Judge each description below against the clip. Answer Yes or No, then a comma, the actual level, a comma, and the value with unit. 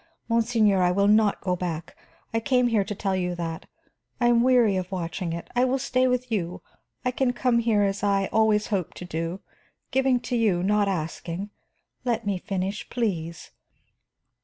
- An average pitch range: Yes, average, 4.6 semitones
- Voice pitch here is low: No, high, 205 Hz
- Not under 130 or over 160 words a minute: No, average, 180 wpm